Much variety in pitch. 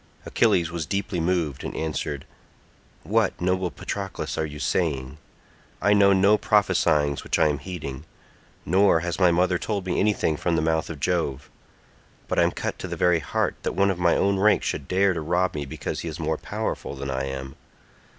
No: average, 3.9 semitones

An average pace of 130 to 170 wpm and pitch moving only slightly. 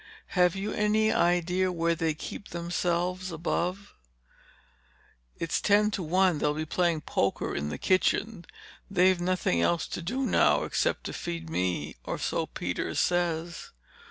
Yes: average, 140 wpm; narrow, 2.2 semitones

